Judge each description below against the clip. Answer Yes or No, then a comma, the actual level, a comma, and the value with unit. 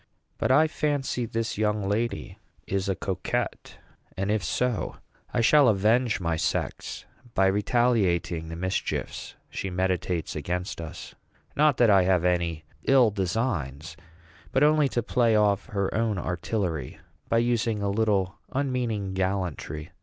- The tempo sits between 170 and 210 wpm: No, average, 140 wpm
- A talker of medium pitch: No, low, 100 Hz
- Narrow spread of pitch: No, average, 4.5 semitones